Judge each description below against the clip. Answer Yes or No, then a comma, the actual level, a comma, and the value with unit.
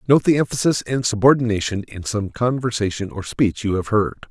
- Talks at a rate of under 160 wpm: No, average, 180 wpm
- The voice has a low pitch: Yes, low, 110 Hz